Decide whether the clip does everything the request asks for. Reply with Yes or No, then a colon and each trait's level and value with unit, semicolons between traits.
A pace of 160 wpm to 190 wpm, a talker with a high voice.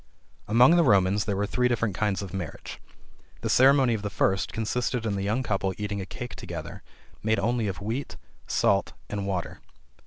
No: average, 185 wpm; low, 105 Hz